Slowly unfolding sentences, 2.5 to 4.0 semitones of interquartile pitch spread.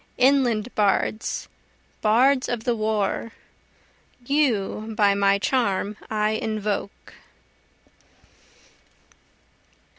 Yes: slow, 70 wpm; average, 2.8 semitones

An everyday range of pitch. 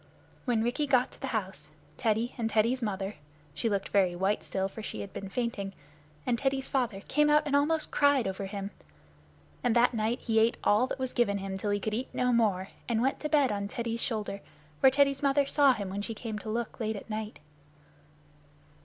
Yes: average, 4.3 semitones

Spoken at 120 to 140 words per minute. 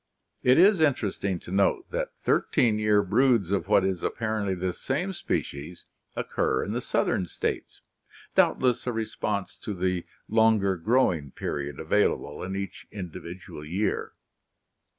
Yes: slow, 135 wpm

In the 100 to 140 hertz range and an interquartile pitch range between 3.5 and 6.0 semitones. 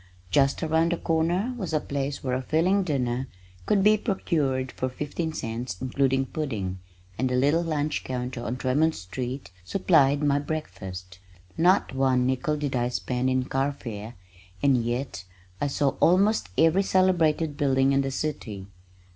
Yes: low, 135 Hz; average, 4.0 semitones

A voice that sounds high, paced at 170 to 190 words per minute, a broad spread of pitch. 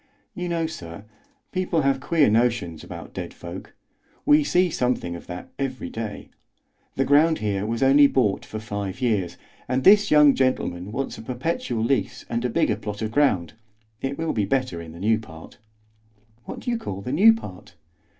No: low, 125 Hz; average, 180 wpm; wide, 6.1 semitones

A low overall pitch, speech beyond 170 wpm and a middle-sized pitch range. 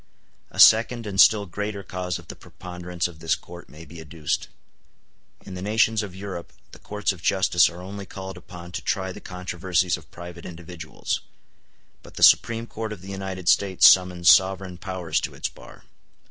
No: very low, 90 Hz; average, 180 wpm; narrow, 2.1 semitones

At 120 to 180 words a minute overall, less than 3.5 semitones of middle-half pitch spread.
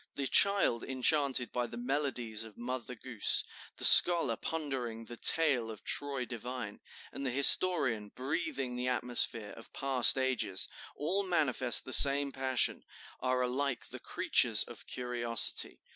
Yes: average, 140 wpm; average, 2.8 semitones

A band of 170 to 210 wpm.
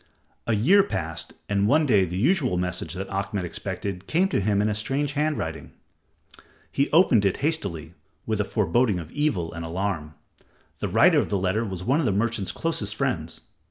Yes: average, 190 wpm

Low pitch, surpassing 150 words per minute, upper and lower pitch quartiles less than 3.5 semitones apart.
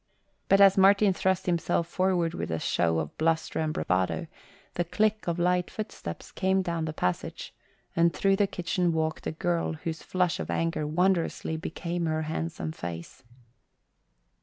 No: medium, 170 Hz; average, 160 wpm; average, 2.8 semitones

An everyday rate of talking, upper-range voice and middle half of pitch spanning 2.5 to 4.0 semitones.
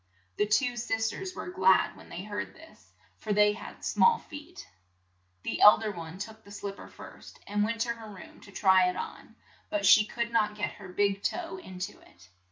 No: fast, 210 wpm; high, 210 Hz; average, 2.9 semitones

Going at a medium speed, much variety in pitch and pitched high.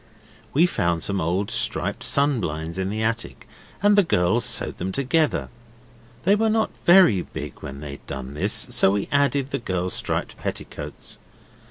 No: average, 165 wpm; wide, 8.7 semitones; low, 105 Hz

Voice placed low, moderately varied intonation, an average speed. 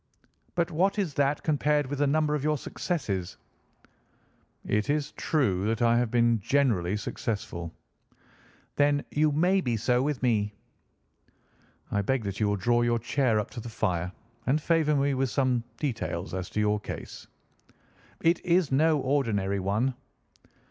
No: low, 130 Hz; wide, 5.7 semitones; average, 155 wpm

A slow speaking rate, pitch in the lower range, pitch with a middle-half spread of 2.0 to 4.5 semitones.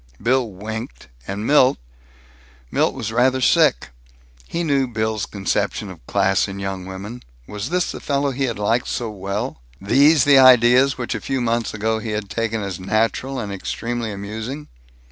No: average, 165 wpm; low, 115 Hz; average, 4.2 semitones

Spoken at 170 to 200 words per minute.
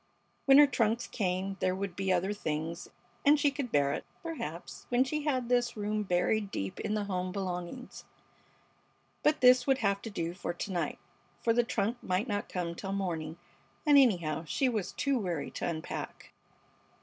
Yes: average, 180 wpm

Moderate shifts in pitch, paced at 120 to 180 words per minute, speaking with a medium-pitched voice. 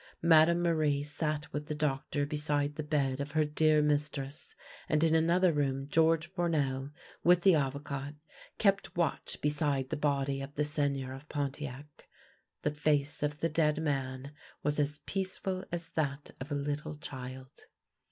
No: narrow, 2.0 semitones; average, 160 wpm; medium, 150 Hz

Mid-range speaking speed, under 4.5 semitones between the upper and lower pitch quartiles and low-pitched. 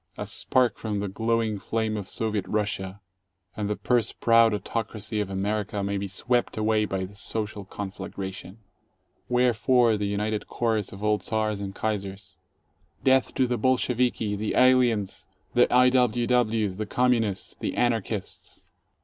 Yes: average, 150 wpm; average, 2.7 semitones; low, 110 Hz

